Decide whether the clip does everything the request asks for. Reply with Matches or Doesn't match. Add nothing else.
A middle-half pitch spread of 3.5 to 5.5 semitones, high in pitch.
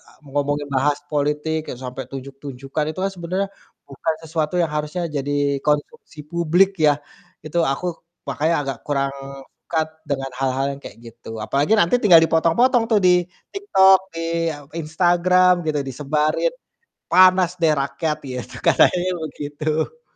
Doesn't match